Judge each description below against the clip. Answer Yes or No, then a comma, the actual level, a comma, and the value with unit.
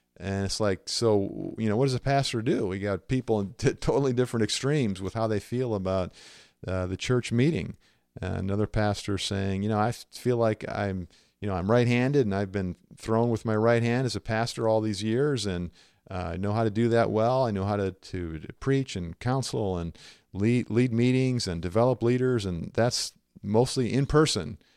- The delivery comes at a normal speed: No, fast, 210 wpm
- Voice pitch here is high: No, low, 110 Hz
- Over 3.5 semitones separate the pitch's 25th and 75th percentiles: Yes, average, 4.1 semitones